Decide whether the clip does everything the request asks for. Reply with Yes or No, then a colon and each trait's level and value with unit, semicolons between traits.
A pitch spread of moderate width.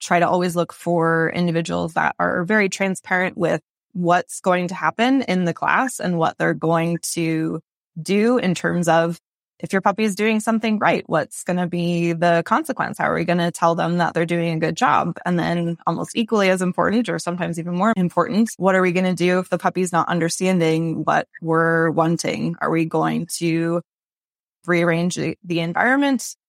No: narrow, 1.9 semitones